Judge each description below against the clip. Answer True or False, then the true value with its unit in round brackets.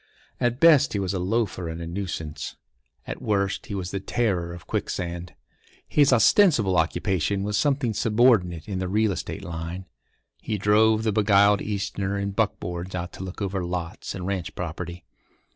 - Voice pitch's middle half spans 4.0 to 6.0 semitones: False (3.4 semitones)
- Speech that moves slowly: False (165 wpm)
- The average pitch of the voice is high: False (95 Hz)